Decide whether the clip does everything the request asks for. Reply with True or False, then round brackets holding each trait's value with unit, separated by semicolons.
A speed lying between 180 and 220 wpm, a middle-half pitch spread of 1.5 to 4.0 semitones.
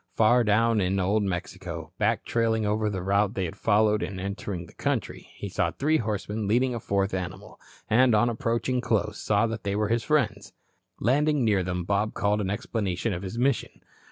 True (185 wpm; 2.8 semitones)